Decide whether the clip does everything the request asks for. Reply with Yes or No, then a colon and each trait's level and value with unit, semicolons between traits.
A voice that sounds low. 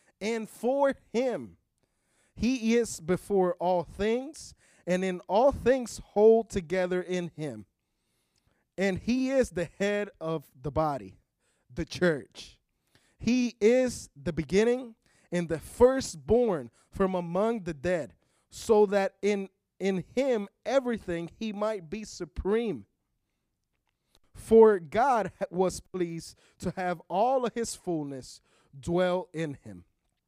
No: high, 190 Hz